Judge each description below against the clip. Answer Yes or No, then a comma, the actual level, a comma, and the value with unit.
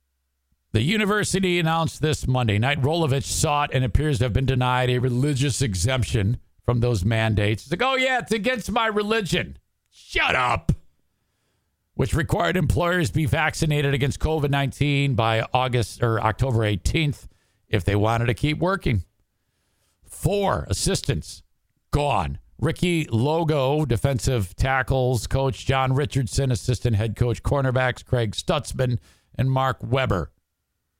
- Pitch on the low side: Yes, low, 130 Hz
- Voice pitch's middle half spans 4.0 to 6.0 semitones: Yes, average, 5.2 semitones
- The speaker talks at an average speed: No, slow, 130 wpm